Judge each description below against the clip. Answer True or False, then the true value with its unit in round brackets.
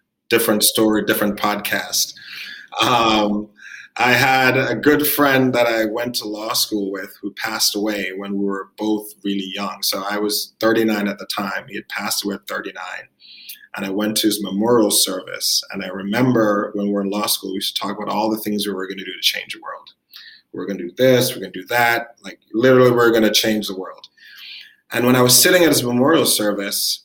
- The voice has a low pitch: True (105 Hz)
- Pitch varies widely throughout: False (2.9 semitones)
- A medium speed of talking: False (225 wpm)